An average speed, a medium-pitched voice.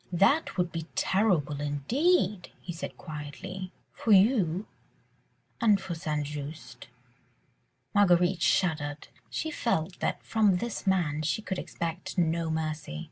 No: slow, 125 wpm; medium, 175 Hz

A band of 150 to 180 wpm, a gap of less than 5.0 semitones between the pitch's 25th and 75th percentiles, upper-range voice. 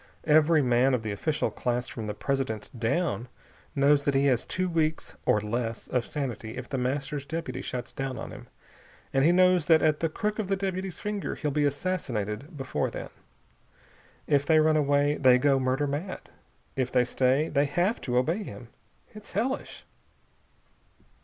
No: average, 175 wpm; average, 4.4 semitones; medium, 145 Hz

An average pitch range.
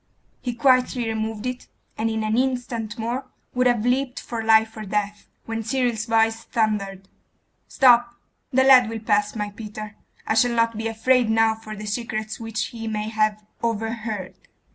No: narrow, 1.9 semitones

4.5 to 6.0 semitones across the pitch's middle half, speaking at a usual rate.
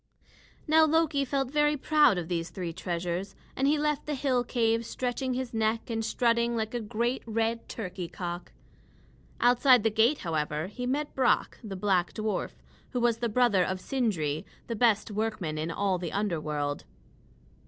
Yes: wide, 5.4 semitones; average, 165 wpm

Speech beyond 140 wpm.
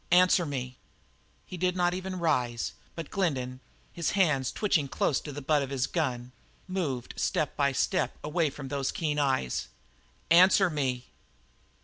Yes: average, 150 wpm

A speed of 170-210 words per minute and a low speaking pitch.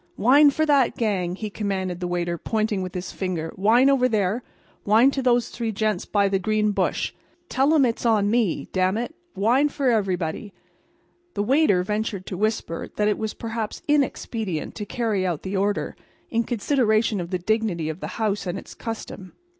No: average, 185 wpm; high, 215 Hz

